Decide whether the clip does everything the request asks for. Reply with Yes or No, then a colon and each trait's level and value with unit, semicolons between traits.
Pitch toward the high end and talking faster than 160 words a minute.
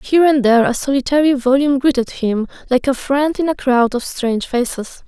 Yes: very high, 265 Hz; average, 200 wpm